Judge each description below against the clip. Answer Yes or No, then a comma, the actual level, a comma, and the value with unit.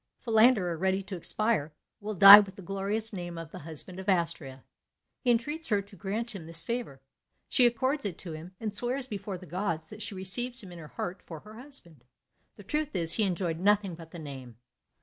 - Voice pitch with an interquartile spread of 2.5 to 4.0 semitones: No, average, 4.7 semitones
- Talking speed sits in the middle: No, fast, 210 wpm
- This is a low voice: No, high, 195 Hz